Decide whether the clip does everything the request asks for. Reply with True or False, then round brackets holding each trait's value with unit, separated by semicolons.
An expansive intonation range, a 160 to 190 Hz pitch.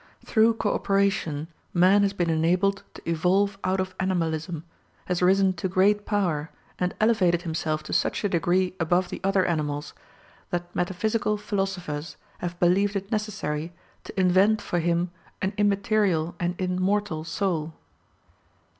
False (2.8 semitones; 185 Hz)